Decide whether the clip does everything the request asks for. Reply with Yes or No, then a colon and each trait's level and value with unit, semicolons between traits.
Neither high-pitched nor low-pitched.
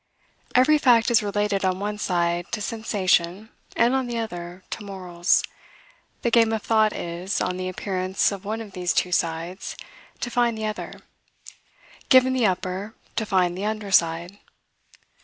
No: high, 200 Hz